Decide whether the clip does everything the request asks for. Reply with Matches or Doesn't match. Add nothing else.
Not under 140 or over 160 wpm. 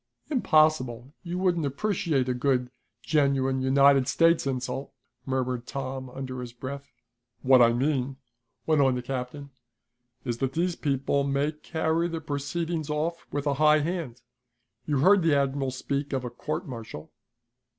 Matches